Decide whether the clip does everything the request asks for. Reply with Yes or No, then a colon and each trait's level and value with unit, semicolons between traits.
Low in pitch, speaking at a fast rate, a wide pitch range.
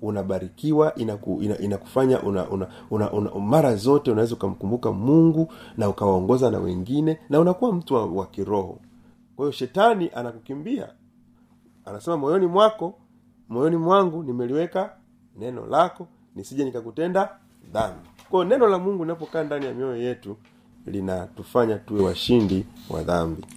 No: low, 125 Hz; average, 130 wpm; wide, 8.2 semitones